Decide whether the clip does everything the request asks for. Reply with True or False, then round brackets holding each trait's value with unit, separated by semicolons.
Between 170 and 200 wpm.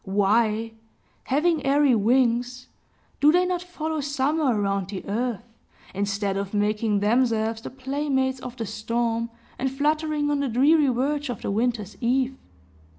False (145 wpm)